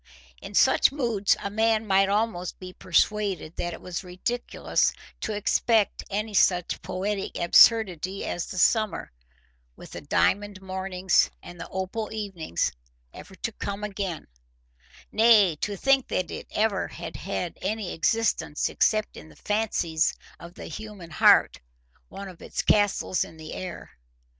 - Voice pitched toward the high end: Yes, high, 195 Hz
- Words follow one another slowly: No, average, 145 wpm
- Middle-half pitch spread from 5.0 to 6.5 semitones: No, average, 3.3 semitones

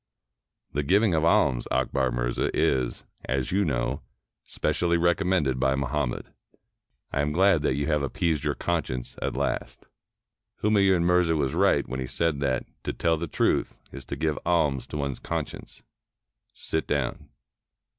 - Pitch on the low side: Yes, very low, 75 Hz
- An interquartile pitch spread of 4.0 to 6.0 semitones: Yes, average, 4.3 semitones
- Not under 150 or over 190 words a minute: Yes, average, 155 wpm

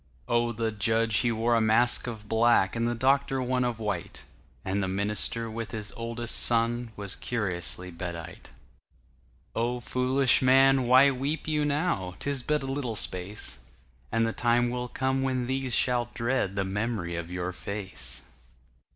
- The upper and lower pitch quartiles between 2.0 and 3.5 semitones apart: No, average, 4.2 semitones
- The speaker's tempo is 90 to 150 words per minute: Yes, average, 140 wpm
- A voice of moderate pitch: No, low, 115 Hz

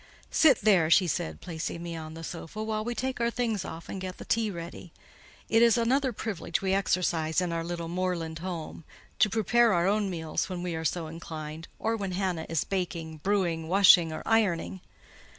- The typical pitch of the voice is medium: Yes, medium, 180 Hz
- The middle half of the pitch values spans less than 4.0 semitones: No, average, 4.5 semitones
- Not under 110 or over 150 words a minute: No, average, 190 wpm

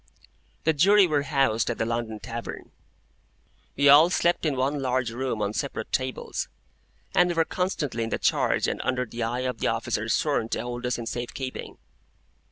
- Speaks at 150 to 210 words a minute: Yes, average, 185 wpm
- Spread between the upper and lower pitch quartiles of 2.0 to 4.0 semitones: Yes, average, 3.7 semitones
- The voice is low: Yes, low, 130 Hz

